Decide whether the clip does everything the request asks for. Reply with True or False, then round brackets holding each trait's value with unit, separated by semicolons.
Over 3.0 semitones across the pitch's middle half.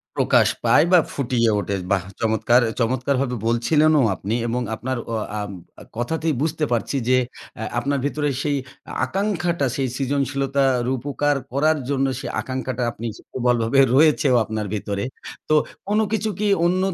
True (4.2 semitones)